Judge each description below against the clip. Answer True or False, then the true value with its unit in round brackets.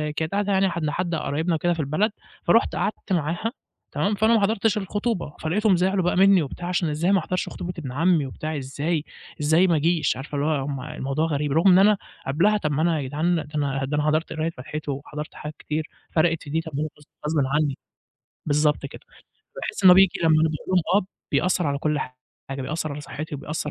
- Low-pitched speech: False (160 Hz)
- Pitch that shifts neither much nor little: True (3.5 semitones)